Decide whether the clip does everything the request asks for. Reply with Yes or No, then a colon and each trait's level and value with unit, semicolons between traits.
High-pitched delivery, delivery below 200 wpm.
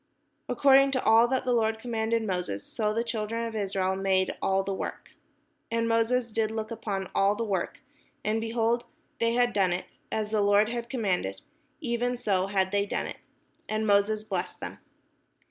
Yes: high, 220 Hz; average, 180 wpm